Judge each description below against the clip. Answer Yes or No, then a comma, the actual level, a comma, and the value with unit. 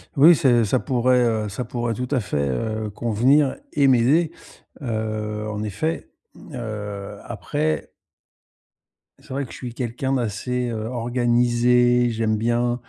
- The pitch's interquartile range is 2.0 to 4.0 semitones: Yes, average, 2.7 semitones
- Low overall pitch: Yes, low, 120 Hz